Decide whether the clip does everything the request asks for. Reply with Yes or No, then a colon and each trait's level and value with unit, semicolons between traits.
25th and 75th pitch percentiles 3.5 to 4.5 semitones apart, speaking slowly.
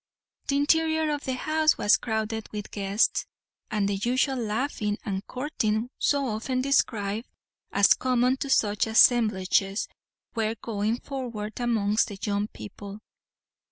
Yes: average, 3.9 semitones; slow, 130 wpm